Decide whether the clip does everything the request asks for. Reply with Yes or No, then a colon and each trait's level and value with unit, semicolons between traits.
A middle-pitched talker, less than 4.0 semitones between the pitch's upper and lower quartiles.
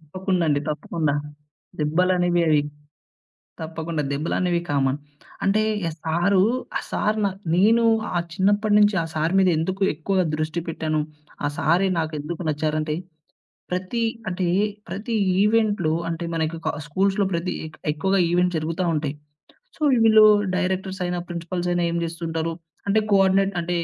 Yes: medium, 175 Hz; average, 3.3 semitones